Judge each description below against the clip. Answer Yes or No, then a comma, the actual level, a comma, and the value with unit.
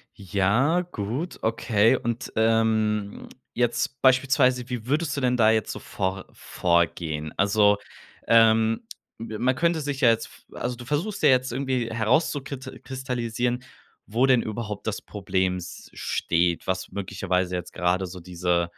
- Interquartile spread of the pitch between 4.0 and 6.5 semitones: Yes, average, 4.7 semitones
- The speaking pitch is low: Yes, low, 115 Hz